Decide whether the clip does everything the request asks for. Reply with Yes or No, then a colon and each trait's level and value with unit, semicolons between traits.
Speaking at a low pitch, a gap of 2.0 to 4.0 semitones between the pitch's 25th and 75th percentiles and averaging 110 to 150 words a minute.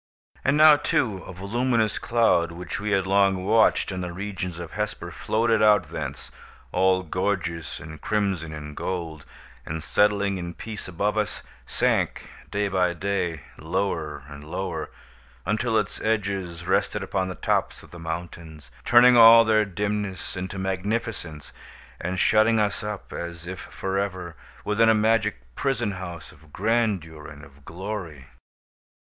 Yes: very low, 95 Hz; average, 3.7 semitones; average, 145 wpm